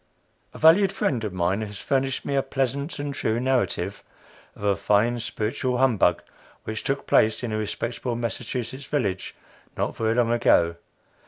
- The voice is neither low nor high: No, low, 120 Hz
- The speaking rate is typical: Yes, average, 160 wpm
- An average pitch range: Yes, average, 3.6 semitones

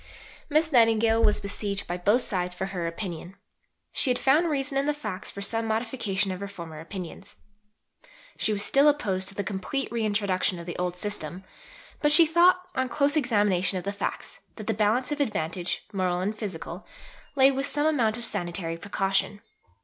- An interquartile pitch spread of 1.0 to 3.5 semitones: No, wide, 5.6 semitones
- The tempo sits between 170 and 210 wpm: Yes, average, 180 wpm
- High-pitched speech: Yes, high, 205 Hz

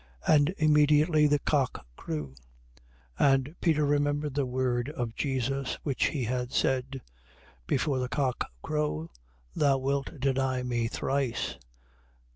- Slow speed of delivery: Yes, slow, 125 wpm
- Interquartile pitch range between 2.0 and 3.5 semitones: Yes, narrow, 2.6 semitones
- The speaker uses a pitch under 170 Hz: Yes, low, 135 Hz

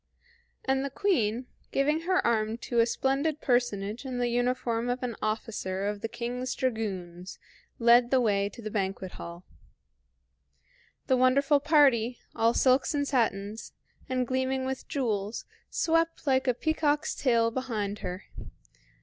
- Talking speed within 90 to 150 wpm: Yes, average, 140 wpm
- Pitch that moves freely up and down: No, average, 3.7 semitones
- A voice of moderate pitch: No, high, 245 Hz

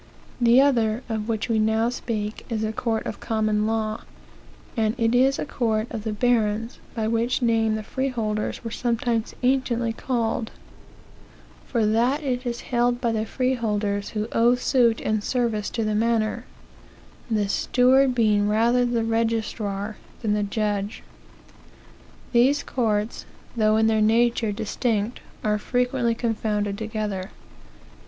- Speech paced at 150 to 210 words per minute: No, average, 140 wpm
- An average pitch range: No, narrow, 2.0 semitones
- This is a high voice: Yes, high, 225 Hz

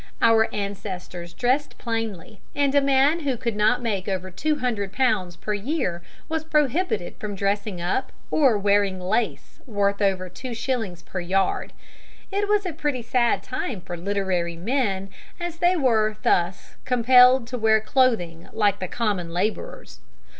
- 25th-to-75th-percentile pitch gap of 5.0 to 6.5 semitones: Yes, wide, 5.4 semitones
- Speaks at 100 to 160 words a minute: Yes, average, 155 wpm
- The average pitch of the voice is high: Yes, high, 215 Hz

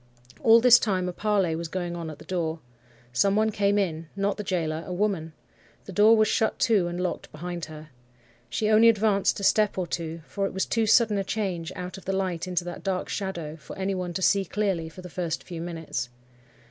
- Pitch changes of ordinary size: Yes, average, 3.3 semitones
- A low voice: No, medium, 185 Hz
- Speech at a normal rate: No, fast, 220 wpm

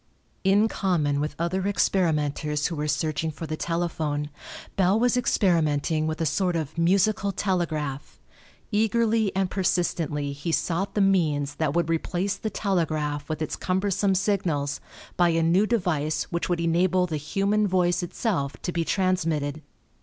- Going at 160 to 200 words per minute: No, average, 150 wpm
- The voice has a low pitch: No, medium, 170 Hz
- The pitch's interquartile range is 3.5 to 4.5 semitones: Yes, average, 4.0 semitones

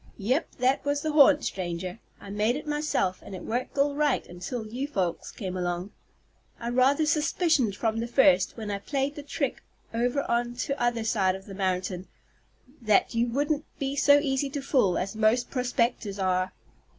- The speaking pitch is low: No, high, 240 Hz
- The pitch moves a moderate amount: No, wide, 6.2 semitones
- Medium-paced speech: Yes, average, 175 wpm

